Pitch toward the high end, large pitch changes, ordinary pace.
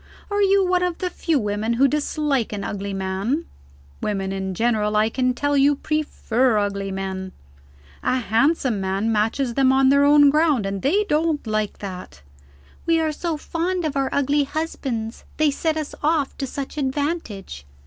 Yes: very high, 265 Hz; wide, 6.5 semitones; average, 170 wpm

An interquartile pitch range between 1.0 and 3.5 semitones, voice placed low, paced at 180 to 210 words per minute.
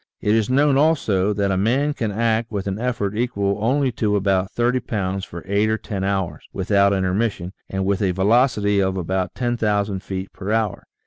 Yes: average, 3.1 semitones; low, 100 Hz; average, 190 wpm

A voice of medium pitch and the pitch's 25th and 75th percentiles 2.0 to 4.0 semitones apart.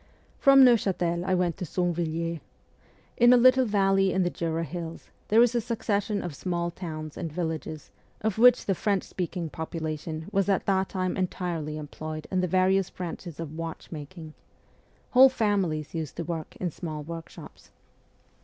Yes: medium, 175 Hz; average, 3.2 semitones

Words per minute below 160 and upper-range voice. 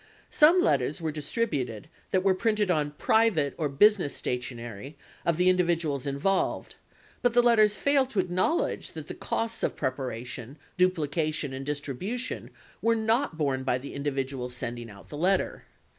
No: average, 150 wpm; medium, 155 Hz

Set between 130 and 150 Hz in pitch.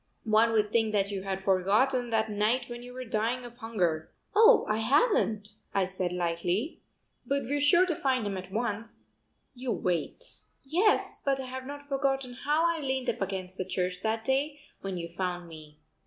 No: high, 225 Hz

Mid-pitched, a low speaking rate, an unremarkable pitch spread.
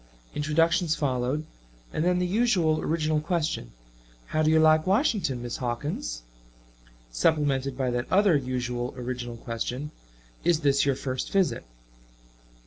Yes: medium, 150 Hz; slow, 130 wpm; average, 4.5 semitones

